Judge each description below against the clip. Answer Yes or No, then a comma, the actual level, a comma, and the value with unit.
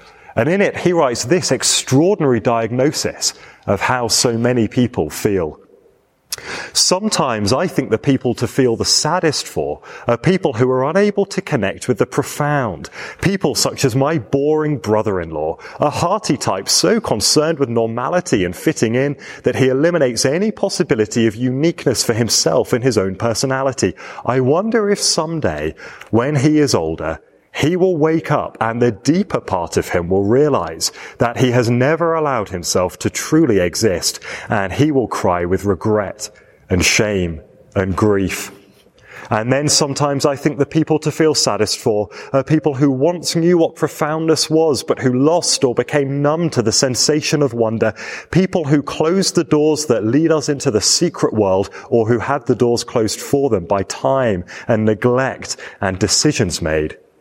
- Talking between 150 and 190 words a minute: Yes, average, 165 wpm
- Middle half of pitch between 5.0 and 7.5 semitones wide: Yes, wide, 5.5 semitones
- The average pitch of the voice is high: No, low, 135 Hz